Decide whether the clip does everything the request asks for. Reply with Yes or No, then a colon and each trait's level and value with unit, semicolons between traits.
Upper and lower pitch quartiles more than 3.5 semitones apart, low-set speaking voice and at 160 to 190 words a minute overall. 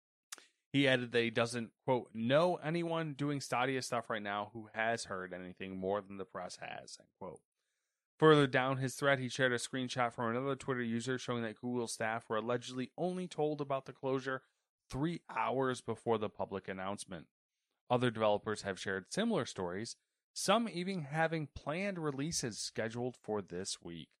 Yes: average, 4.4 semitones; low, 125 Hz; average, 170 wpm